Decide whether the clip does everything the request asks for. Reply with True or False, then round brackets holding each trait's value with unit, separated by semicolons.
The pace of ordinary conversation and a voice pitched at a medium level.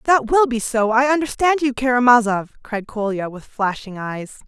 False (175 wpm; 240 Hz)